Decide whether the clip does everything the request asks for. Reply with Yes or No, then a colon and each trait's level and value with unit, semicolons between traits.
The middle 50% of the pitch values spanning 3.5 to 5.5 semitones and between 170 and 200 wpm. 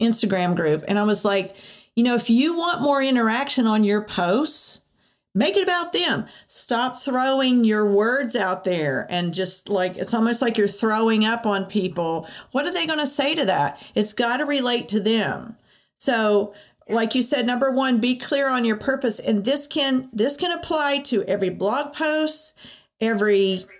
Yes: average, 4.8 semitones; average, 185 wpm